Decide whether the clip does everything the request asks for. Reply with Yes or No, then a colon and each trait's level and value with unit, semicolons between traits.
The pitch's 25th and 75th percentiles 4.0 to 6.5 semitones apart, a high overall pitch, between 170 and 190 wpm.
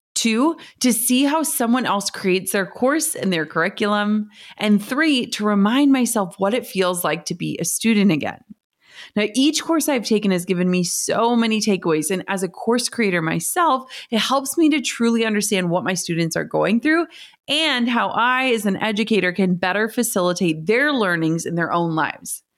Yes: average, 5.2 semitones; high, 215 Hz; average, 185 wpm